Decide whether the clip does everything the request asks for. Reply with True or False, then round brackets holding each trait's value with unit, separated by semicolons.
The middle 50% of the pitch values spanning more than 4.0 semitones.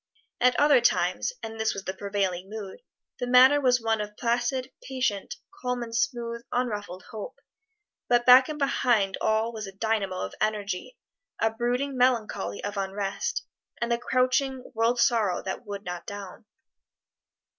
False (3.6 semitones)